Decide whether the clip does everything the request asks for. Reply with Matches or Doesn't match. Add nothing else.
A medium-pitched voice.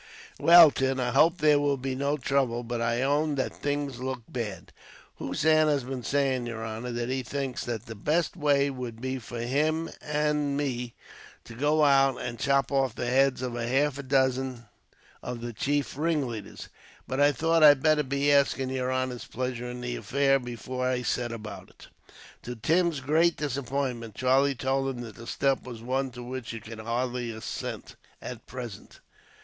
Doesn't match